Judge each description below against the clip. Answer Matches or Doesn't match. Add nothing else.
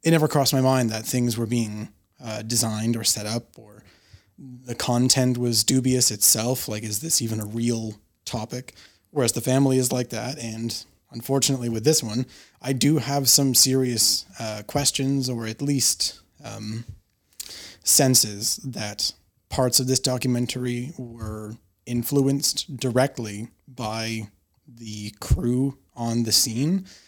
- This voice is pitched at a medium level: Doesn't match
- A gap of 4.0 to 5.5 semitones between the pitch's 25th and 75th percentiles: Doesn't match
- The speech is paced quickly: Doesn't match